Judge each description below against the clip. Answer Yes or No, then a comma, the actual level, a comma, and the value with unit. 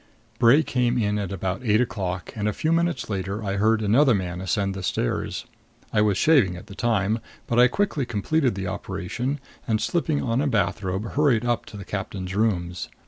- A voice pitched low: Yes, low, 105 Hz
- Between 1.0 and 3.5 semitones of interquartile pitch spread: No, average, 4.3 semitones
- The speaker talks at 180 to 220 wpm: Yes, average, 190 wpm